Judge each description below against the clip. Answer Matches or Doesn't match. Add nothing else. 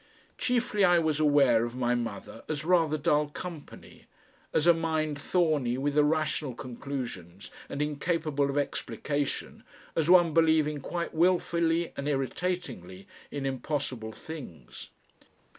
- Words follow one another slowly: Matches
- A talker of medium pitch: Matches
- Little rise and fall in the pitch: Doesn't match